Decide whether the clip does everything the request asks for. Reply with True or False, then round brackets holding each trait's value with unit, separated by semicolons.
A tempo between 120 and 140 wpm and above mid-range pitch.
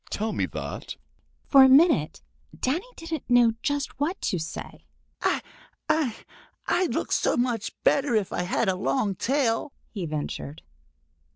True (135 wpm; 250 Hz)